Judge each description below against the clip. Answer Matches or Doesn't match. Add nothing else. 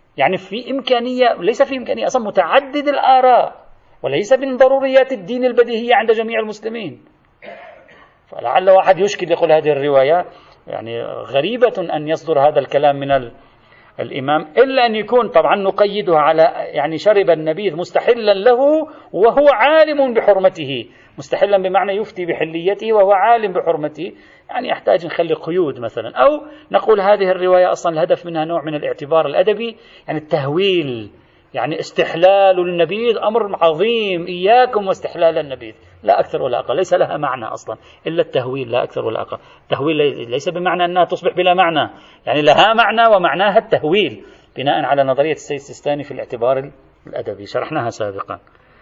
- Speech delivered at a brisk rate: Matches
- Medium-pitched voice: Doesn't match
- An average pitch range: Doesn't match